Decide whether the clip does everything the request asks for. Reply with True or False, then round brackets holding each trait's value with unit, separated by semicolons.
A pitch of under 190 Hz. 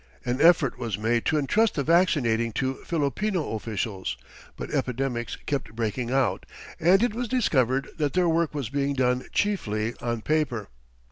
True (135 Hz)